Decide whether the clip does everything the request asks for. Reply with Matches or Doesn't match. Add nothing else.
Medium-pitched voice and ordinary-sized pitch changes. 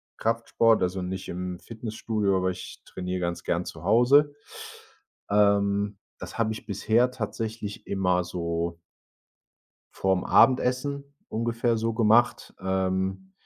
Doesn't match